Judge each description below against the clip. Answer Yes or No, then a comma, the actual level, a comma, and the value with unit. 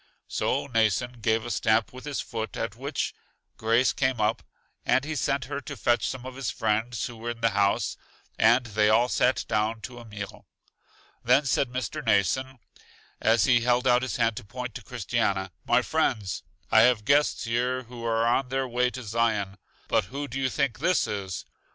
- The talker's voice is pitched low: Yes, low, 120 Hz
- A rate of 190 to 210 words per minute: Yes, average, 195 wpm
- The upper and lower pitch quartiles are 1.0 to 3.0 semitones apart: Yes, average, 2.7 semitones